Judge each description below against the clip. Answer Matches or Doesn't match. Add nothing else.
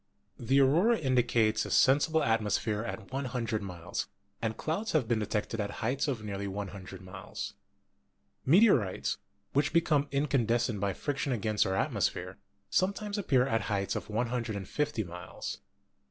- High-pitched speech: Doesn't match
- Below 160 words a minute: Matches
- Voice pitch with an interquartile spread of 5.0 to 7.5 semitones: Matches